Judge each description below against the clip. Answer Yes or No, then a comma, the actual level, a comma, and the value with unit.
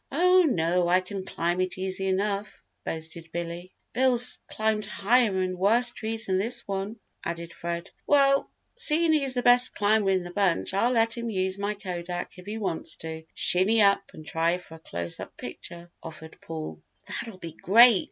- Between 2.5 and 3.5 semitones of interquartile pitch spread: No, average, 4.8 semitones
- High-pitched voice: Yes, high, 195 Hz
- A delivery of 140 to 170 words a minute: No, average, 180 wpm